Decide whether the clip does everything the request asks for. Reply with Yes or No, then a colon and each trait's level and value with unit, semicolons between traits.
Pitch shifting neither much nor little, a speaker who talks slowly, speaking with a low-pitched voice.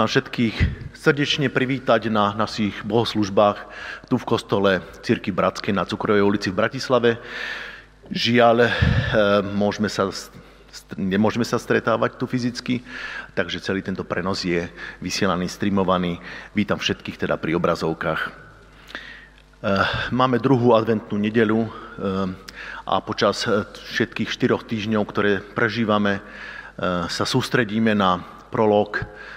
Yes: average, 3.0 semitones; slow, 100 wpm; low, 105 Hz